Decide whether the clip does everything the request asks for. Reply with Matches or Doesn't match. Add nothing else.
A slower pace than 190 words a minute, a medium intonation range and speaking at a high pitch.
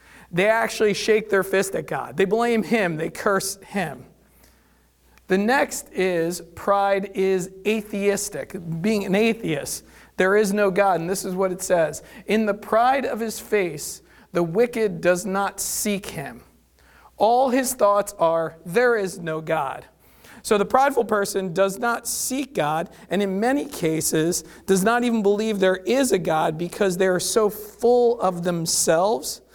Matches